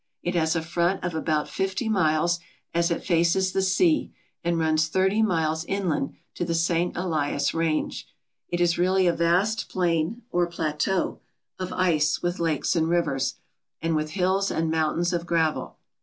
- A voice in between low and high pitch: Yes, medium, 170 Hz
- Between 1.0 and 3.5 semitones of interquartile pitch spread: Yes, narrow, 2.4 semitones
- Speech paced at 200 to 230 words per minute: No, average, 165 wpm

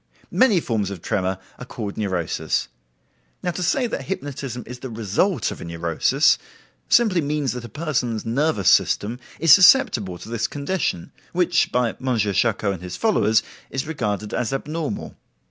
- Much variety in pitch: Yes, wide, 7.3 semitones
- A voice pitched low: Yes, low, 125 Hz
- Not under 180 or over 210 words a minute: No, average, 160 wpm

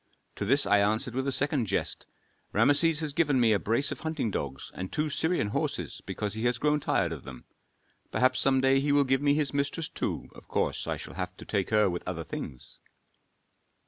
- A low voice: Yes, low, 130 Hz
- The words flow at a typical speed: No, fast, 210 wpm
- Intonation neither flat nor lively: No, wide, 5.9 semitones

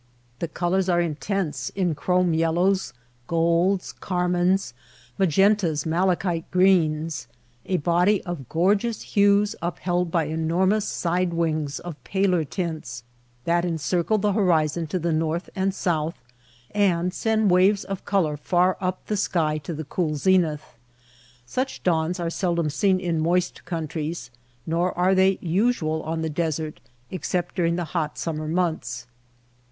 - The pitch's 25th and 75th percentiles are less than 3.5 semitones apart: Yes, average, 2.8 semitones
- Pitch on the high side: No, medium, 175 Hz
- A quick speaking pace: No, average, 145 wpm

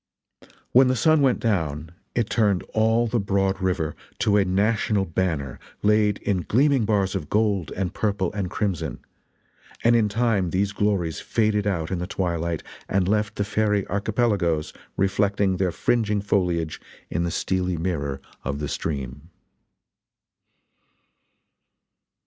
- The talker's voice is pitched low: Yes, low, 100 Hz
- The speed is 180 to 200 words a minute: No, slow, 135 wpm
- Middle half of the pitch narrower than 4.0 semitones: Yes, average, 3.6 semitones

